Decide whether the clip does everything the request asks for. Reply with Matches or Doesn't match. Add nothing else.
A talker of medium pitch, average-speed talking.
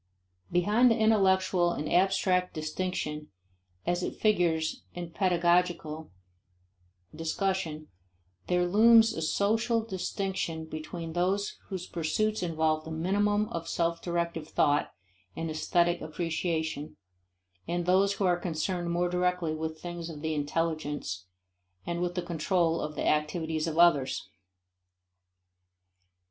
Doesn't match